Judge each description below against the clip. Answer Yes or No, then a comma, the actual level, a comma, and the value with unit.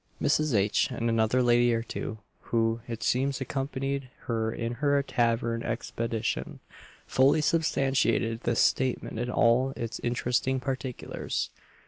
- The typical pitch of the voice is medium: No, low, 120 Hz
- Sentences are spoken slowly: Yes, slow, 125 wpm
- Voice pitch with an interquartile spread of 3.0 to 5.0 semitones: No, narrow, 2.5 semitones